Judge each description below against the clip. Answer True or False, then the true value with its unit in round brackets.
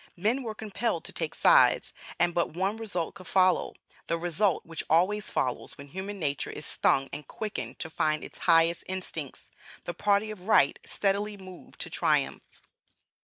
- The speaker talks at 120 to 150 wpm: False (170 wpm)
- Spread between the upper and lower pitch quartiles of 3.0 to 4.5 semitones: True (4.0 semitones)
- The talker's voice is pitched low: False (185 Hz)